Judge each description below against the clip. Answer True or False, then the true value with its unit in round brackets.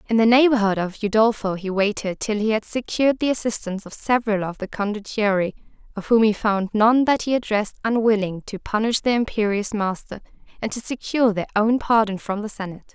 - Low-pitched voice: False (215 Hz)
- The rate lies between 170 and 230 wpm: True (190 wpm)